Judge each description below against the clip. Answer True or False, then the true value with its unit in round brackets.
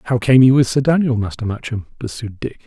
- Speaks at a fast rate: True (250 wpm)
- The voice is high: False (120 Hz)